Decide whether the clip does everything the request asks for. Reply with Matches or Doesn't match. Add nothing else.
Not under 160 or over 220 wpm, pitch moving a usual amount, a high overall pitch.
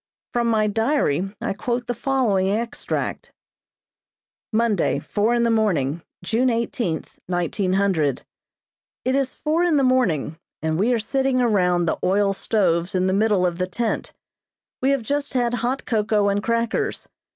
Doesn't match